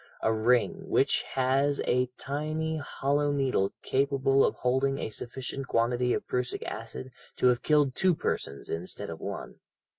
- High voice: No, low, 135 Hz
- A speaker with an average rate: Yes, average, 150 wpm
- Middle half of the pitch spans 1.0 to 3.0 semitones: Yes, narrow, 2.5 semitones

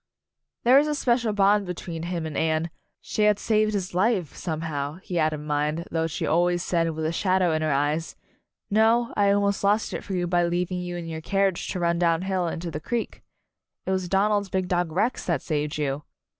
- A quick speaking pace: Yes, fast, 225 wpm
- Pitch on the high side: No, medium, 175 Hz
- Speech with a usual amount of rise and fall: Yes, average, 3.7 semitones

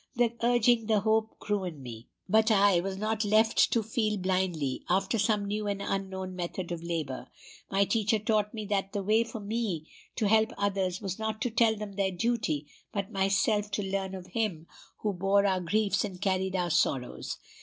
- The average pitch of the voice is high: Yes, high, 200 Hz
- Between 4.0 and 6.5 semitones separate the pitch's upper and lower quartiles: No, narrow, 2.6 semitones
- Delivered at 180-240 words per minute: Yes, average, 190 wpm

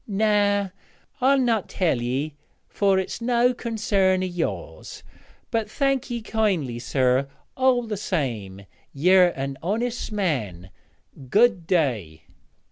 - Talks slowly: Yes, slow, 120 wpm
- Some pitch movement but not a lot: No, wide, 8.4 semitones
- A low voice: No, high, 190 Hz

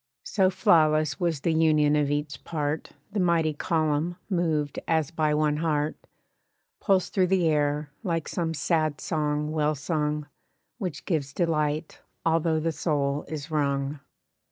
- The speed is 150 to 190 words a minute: No, average, 140 wpm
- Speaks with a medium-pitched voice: Yes, medium, 155 Hz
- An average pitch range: No, narrow, 2.0 semitones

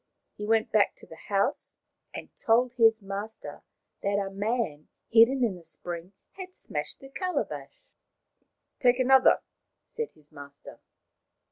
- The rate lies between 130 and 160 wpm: Yes, average, 140 wpm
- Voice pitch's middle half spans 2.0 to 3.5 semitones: No, average, 4.4 semitones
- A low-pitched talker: No, high, 220 Hz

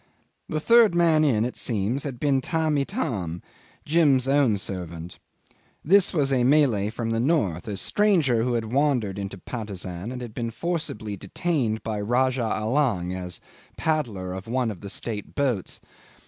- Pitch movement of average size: No, wide, 6.1 semitones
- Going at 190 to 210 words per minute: No, average, 160 wpm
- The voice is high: No, low, 120 Hz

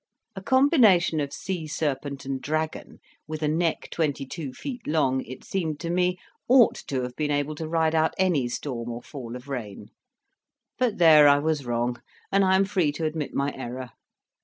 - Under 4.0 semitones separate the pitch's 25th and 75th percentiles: No, average, 4.4 semitones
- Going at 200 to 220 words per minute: No, average, 185 wpm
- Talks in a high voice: No, medium, 155 Hz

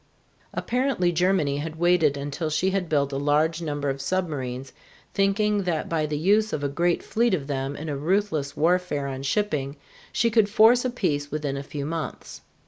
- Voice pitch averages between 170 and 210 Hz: No, medium, 160 Hz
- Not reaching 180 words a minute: No, average, 185 wpm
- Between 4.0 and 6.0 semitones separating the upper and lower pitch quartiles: Yes, average, 5.0 semitones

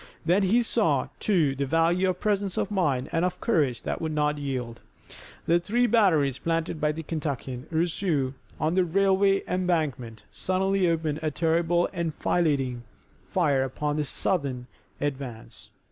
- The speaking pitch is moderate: Yes, medium, 160 Hz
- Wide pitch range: No, average, 4.6 semitones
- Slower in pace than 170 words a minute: Yes, average, 150 wpm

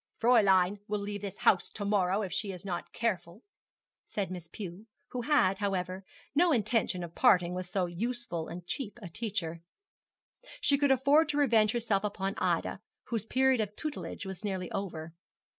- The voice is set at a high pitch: Yes, high, 200 Hz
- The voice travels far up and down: No, average, 4.3 semitones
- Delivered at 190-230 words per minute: No, average, 170 wpm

